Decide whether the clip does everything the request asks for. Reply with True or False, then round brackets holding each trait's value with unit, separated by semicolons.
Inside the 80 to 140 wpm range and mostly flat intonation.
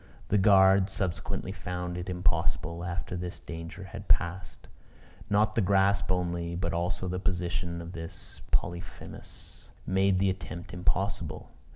True (135 wpm; 1.8 semitones)